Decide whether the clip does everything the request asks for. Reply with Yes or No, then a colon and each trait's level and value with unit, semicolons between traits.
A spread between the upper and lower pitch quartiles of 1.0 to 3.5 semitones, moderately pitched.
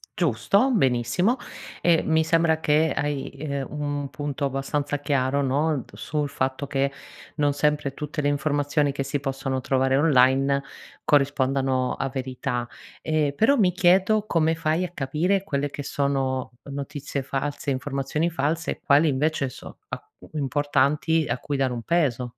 Yes: narrow, 2.6 semitones; medium, 145 Hz